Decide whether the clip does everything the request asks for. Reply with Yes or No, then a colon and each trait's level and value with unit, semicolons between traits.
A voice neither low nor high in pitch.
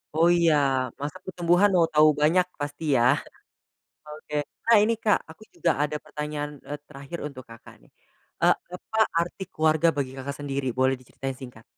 Yes: medium, 150 Hz